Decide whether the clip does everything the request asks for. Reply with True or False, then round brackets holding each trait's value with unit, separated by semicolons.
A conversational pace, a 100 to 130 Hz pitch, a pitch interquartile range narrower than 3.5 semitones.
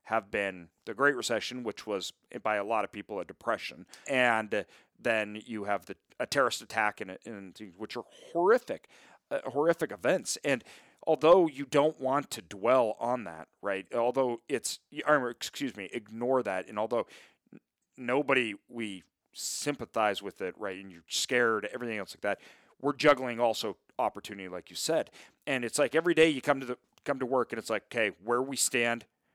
False (180 wpm; 120 Hz; 5.0 semitones)